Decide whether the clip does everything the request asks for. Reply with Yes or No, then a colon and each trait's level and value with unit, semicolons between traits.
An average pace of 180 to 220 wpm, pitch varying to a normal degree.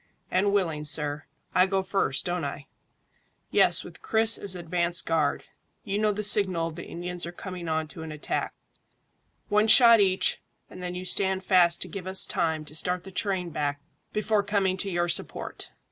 Yes: average, 185 wpm; average, 3.0 semitones